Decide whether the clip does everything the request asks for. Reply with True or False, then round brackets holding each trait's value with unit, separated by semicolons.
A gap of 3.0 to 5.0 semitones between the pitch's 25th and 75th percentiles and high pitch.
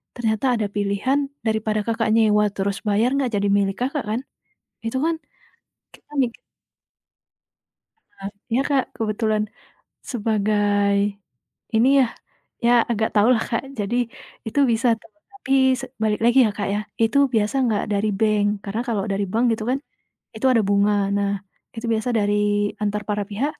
False (2.6 semitones; 215 Hz)